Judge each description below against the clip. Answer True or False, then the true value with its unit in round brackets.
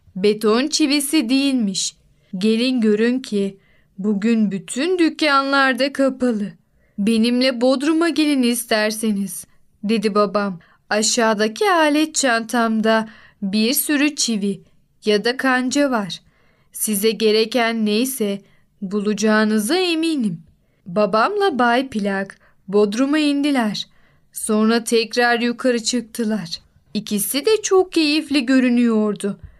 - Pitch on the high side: True (230 Hz)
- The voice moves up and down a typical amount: True (4.2 semitones)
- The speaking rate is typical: False (90 wpm)